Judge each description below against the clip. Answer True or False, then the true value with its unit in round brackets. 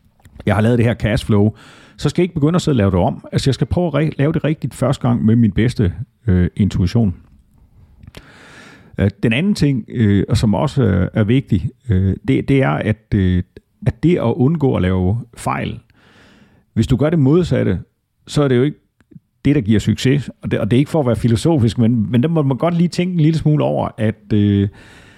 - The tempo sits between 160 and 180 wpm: False (220 wpm)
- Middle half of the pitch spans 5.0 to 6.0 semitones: True (5.5 semitones)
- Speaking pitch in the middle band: False (115 Hz)